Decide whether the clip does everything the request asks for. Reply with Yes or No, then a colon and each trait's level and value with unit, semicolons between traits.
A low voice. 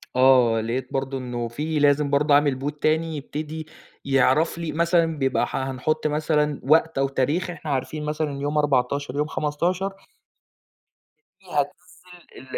No: medium, 145 Hz